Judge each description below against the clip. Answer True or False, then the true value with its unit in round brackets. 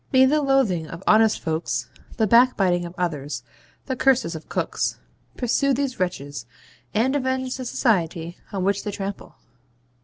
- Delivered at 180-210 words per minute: False (150 wpm)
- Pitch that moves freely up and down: True (7.5 semitones)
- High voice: True (200 Hz)